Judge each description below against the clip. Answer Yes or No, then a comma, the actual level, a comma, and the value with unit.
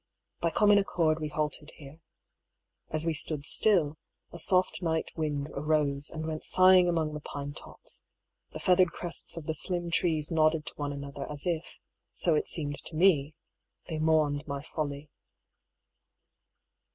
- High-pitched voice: No, medium, 155 Hz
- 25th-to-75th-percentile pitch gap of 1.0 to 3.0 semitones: Yes, narrow, 2.4 semitones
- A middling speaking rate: Yes, average, 155 wpm